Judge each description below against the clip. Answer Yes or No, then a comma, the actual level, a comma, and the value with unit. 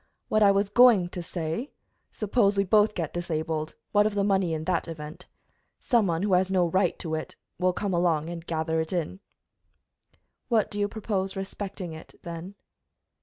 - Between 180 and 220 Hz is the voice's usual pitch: Yes, medium, 185 Hz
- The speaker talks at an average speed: Yes, average, 180 wpm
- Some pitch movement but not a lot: Yes, average, 3.6 semitones